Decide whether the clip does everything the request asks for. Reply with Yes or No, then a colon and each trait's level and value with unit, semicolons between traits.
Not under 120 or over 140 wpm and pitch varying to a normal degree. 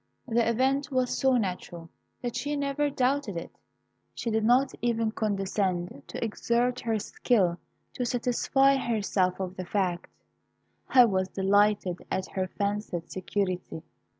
Yes: slow, 135 wpm; average, 4.8 semitones